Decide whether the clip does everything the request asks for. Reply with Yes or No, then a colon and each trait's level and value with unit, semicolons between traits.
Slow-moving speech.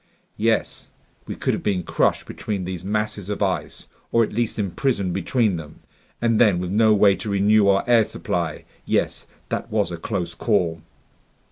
No: average, 170 wpm